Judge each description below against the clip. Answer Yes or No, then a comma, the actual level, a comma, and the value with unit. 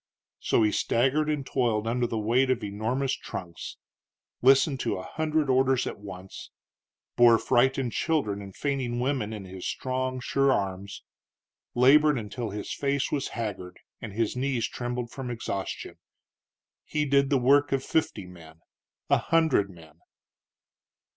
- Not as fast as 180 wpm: Yes, average, 145 wpm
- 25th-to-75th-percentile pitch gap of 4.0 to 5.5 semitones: Yes, average, 4.7 semitones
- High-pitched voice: No, low, 125 Hz